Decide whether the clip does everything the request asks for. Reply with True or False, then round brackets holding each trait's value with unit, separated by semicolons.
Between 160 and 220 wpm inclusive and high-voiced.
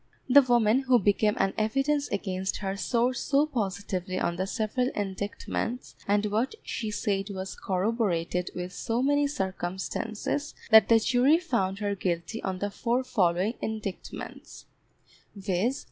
False (140 wpm; 210 Hz)